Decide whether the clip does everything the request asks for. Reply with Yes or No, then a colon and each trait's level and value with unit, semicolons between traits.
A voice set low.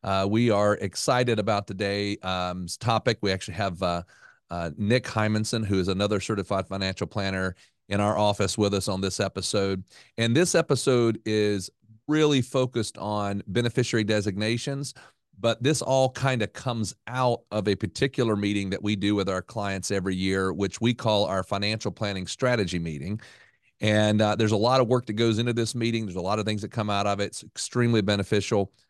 Yes: low, 105 Hz